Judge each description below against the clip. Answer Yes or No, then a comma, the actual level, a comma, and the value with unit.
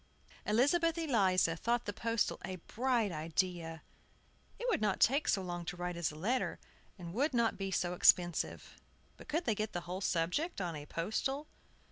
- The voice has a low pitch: No, high, 195 Hz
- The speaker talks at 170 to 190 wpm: Yes, average, 175 wpm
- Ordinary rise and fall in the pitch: No, wide, 5.7 semitones